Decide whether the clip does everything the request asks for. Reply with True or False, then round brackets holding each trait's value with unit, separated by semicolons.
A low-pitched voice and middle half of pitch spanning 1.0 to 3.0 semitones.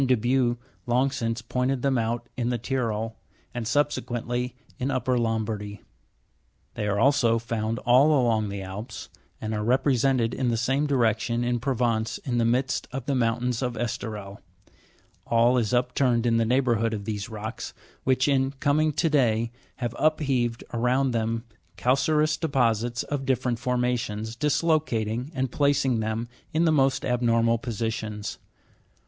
True (120 Hz; 2.7 semitones)